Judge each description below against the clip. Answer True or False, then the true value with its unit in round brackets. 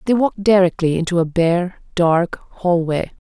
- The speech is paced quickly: False (145 wpm)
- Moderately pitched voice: True (180 Hz)